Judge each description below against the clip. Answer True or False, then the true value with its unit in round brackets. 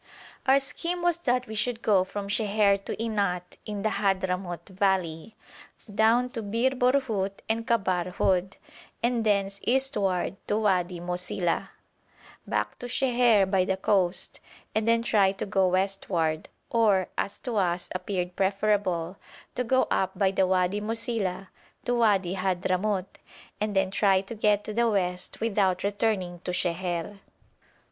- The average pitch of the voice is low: False (200 Hz)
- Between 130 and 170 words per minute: True (150 wpm)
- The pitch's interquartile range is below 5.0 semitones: True (3.2 semitones)